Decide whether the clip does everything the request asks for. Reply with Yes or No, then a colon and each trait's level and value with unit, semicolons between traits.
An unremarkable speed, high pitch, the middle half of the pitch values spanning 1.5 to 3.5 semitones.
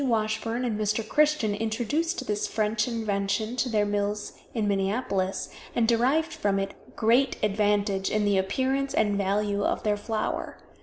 Yes: average, 150 wpm; high, 215 Hz; average, 2.8 semitones